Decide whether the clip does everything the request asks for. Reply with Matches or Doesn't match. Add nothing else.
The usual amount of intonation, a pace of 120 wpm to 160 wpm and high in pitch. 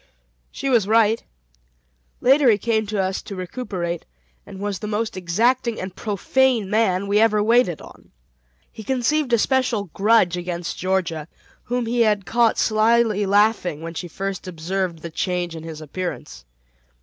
Matches